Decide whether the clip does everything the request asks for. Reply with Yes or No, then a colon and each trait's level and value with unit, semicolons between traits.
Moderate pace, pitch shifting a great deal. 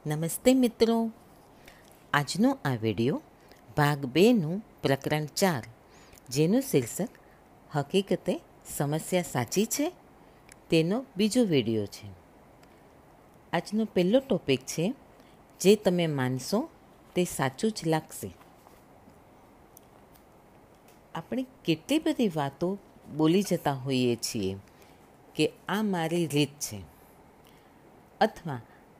Yes: average, 90 wpm; wide, 7.7 semitones